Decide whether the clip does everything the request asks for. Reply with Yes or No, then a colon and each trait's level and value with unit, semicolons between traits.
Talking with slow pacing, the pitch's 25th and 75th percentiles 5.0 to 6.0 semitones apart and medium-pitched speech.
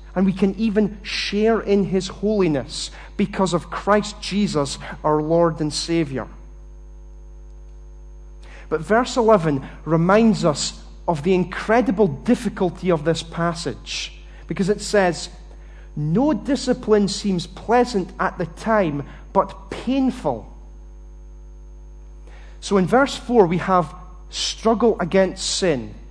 Yes: slow, 115 wpm; wide, 5.4 semitones; medium, 180 Hz